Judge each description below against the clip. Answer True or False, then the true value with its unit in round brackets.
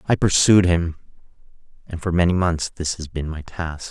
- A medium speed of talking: True (185 wpm)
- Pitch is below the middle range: True (85 Hz)